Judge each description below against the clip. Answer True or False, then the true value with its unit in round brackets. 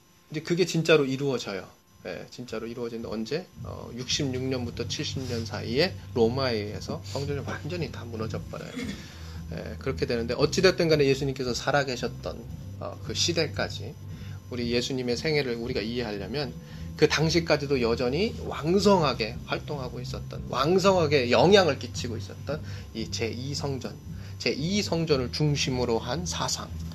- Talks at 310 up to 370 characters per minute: True (315 characters per minute)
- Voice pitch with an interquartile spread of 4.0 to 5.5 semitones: False (6.1 semitones)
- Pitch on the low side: True (120 Hz)